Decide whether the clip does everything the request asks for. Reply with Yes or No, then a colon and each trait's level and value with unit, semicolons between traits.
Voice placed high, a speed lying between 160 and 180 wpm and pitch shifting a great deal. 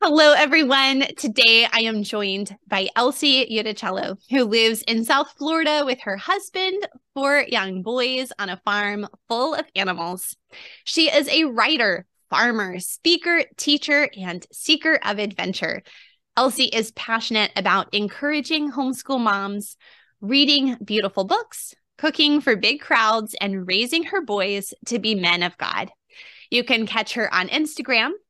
No: high, 240 Hz; average, 140 wpm; wide, 6.2 semitones